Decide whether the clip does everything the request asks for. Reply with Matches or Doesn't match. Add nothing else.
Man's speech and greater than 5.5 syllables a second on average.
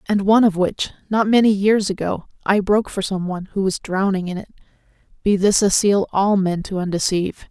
Doesn't match